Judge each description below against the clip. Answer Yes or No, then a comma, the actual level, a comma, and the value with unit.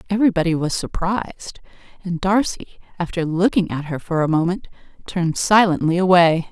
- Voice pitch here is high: No, medium, 175 Hz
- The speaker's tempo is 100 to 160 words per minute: Yes, average, 140 wpm